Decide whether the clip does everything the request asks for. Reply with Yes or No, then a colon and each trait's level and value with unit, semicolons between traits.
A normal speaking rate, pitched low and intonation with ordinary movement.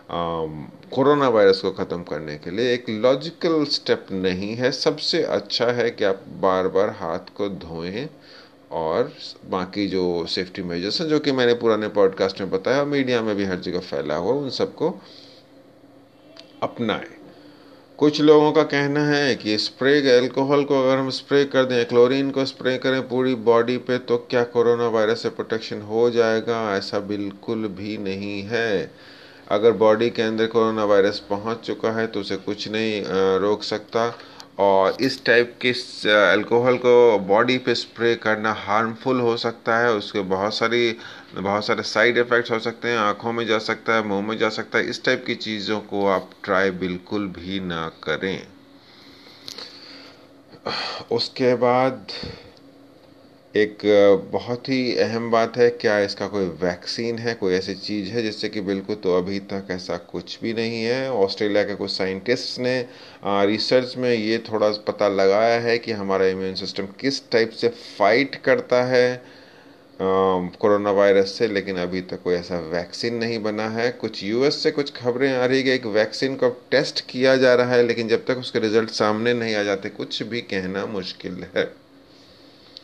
Yes: average, 170 wpm; low, 115 Hz; average, 3.7 semitones